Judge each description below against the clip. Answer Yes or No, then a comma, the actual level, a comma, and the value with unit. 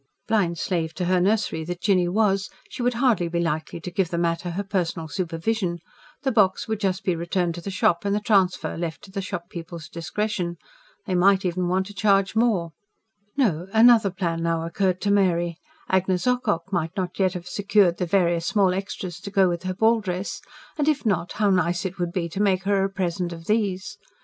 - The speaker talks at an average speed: No, fast, 210 wpm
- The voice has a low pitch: No, medium, 185 Hz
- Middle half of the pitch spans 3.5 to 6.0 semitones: No, average, 2.9 semitones